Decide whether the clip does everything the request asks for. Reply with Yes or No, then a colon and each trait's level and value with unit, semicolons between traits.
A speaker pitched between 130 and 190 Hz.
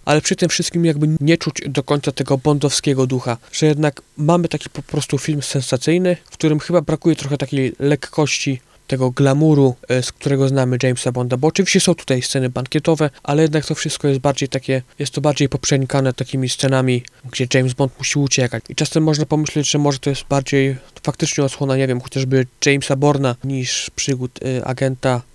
Yes: medium, 140 Hz